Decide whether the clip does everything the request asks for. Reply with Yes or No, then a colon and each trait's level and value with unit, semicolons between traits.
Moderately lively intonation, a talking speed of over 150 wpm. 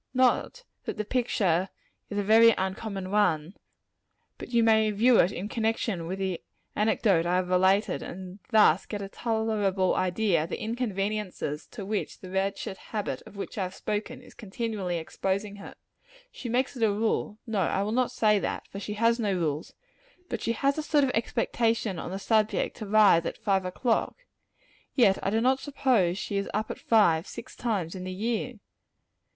Yes: average, 3.2 semitones; average, 190 wpm